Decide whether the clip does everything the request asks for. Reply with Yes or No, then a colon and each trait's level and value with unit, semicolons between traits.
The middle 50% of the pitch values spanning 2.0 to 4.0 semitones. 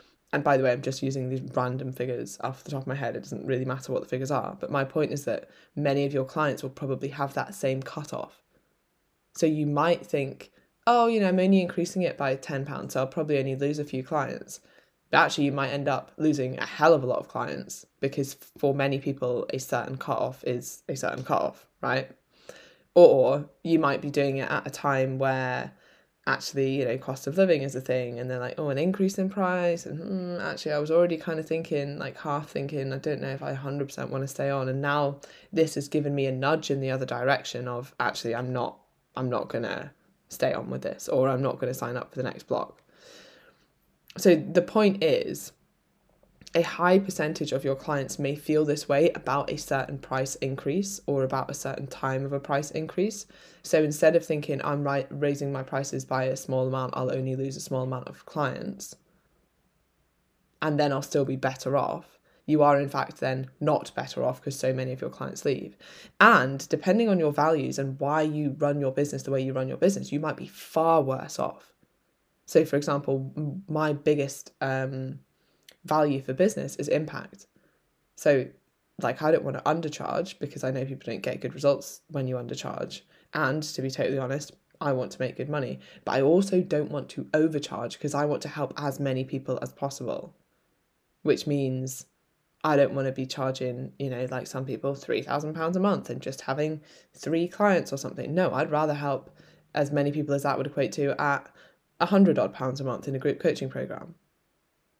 Yes: average, 2.7 semitones